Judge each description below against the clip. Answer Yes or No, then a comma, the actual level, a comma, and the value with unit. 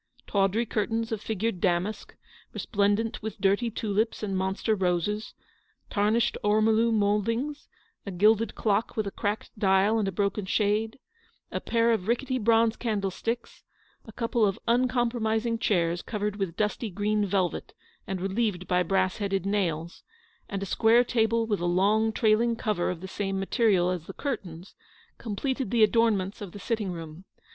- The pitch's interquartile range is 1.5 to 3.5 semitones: Yes, average, 2.8 semitones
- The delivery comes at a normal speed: Yes, average, 165 wpm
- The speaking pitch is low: No, high, 210 Hz